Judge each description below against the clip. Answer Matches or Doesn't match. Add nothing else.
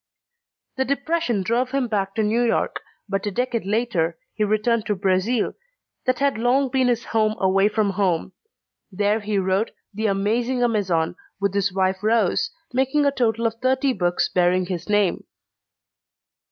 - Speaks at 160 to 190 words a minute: Matches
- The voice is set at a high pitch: Matches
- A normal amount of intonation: Matches